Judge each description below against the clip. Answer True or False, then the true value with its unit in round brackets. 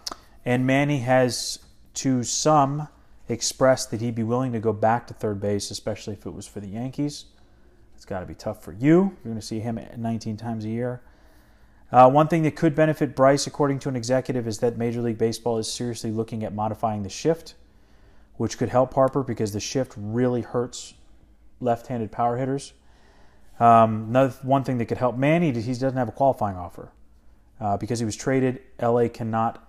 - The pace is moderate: True (195 wpm)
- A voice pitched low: True (120 Hz)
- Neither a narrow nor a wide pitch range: True (3.0 semitones)